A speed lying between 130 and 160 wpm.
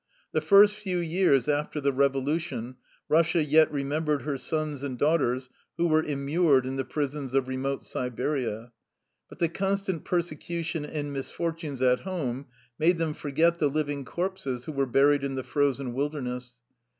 Yes: average, 155 wpm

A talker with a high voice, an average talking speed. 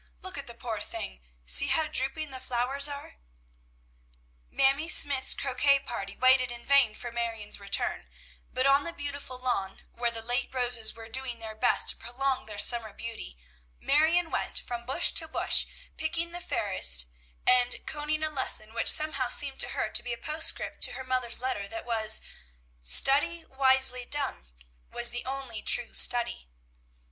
Yes: very high, 255 Hz; average, 165 wpm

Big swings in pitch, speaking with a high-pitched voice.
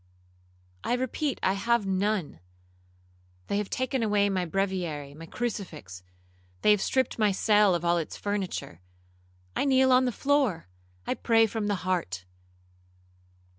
Yes: wide, 6.2 semitones; high, 195 Hz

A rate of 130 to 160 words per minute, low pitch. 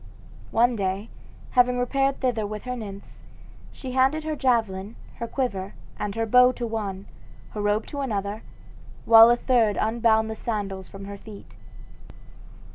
No: average, 150 wpm; high, 225 Hz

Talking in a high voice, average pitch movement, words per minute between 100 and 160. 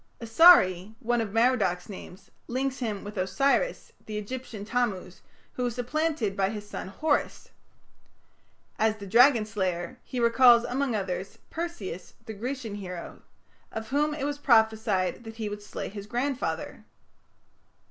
Yes: high, 220 Hz; average, 4.2 semitones; average, 140 wpm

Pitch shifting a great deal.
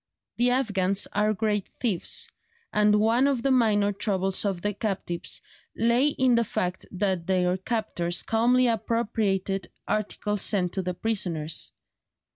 No: average, 3.4 semitones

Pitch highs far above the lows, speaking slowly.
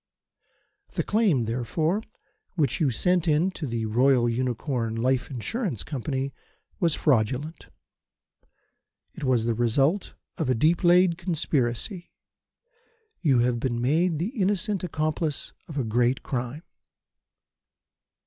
Yes: wide, 5.9 semitones; slow, 120 wpm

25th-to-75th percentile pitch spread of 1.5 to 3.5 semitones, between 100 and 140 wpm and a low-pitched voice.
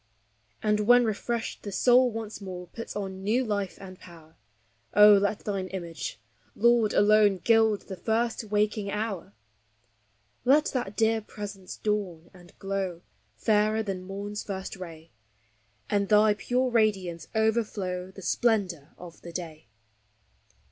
No: average, 3.0 semitones; slow, 135 wpm; high, 205 Hz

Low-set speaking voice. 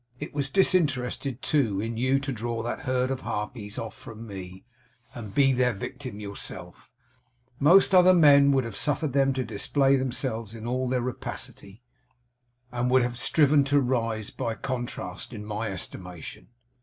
Yes: low, 125 Hz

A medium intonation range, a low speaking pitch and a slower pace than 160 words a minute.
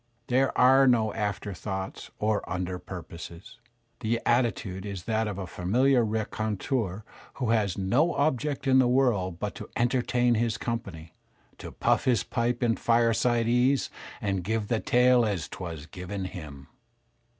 Yes: average, 4.3 semitones; low, 110 Hz; average, 150 wpm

